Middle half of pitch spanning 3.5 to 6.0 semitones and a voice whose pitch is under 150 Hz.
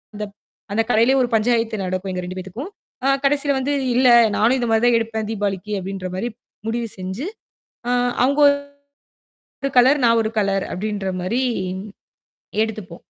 No: average, 4.1 semitones; high, 220 Hz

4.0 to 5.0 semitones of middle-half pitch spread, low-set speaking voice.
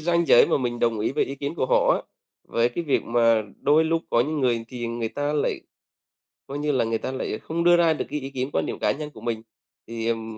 Yes: average, 4.4 semitones; low, 130 Hz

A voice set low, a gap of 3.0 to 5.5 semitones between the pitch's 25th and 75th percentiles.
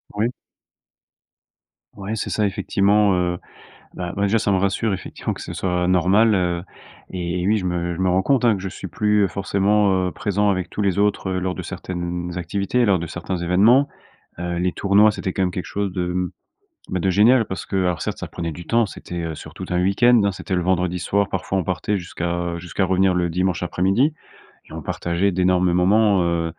No: very low, 95 Hz; narrow, 2.4 semitones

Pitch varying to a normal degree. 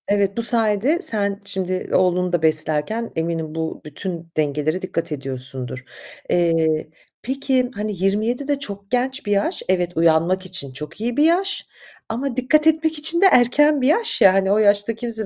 No: wide, 7.0 semitones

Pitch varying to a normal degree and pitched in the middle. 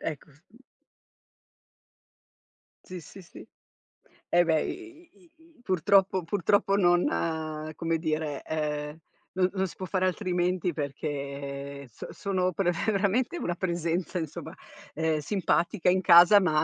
Yes: average, 3.6 semitones; medium, 175 Hz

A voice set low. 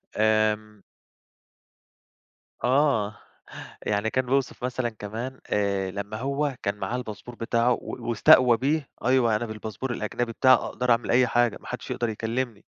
Yes: low, 115 Hz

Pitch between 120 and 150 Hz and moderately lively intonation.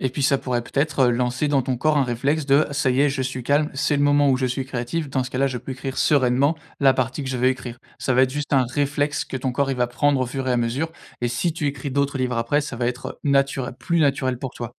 No: low, 135 Hz; narrow, 2.3 semitones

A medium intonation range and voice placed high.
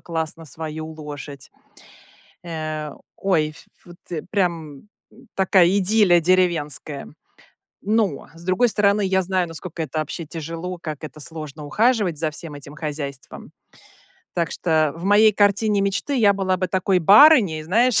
No: average, 4.2 semitones; medium, 175 Hz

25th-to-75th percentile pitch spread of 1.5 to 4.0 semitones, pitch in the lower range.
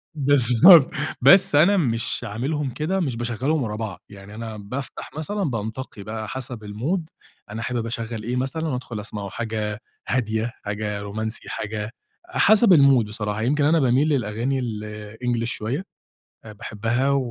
No: average, 4.4 semitones; low, 120 Hz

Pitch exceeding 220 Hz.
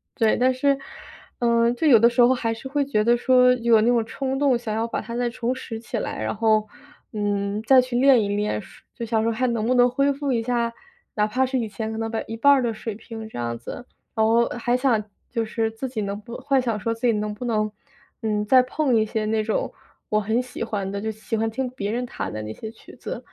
Yes: high, 230 Hz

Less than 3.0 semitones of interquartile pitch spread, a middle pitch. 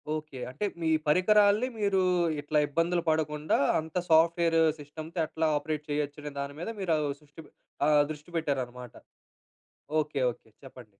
Yes: narrow, 2.4 semitones; medium, 155 Hz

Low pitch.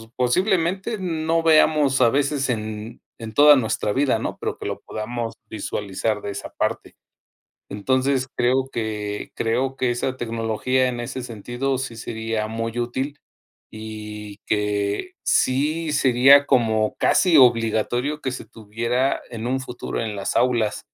Yes: low, 120 Hz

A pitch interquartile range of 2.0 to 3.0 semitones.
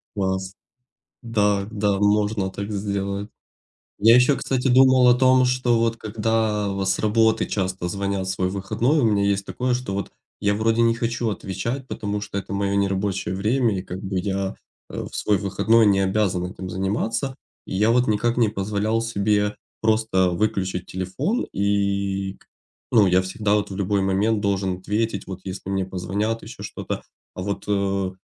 Yes: narrow, 2.6 semitones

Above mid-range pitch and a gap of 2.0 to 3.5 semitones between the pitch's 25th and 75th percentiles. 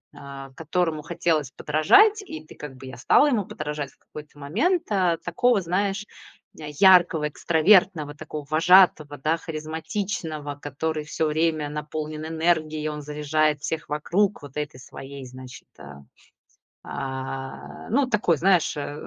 No: medium, 155 Hz; average, 3.2 semitones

